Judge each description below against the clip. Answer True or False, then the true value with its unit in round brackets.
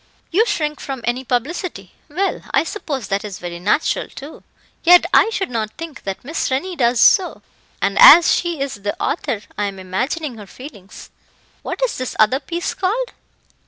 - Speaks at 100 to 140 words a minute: False (175 wpm)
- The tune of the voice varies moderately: False (8.1 semitones)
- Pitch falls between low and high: False (275 Hz)